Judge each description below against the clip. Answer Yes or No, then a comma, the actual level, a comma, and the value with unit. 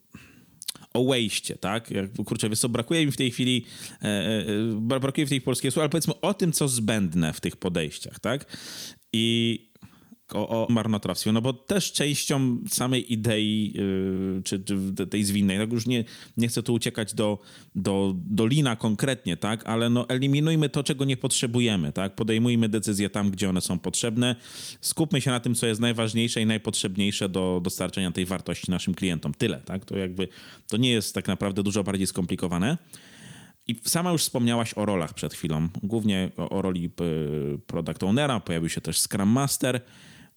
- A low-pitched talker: Yes, low, 110 Hz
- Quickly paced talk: Yes, fast, 175 wpm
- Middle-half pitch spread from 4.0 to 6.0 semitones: Yes, average, 4.4 semitones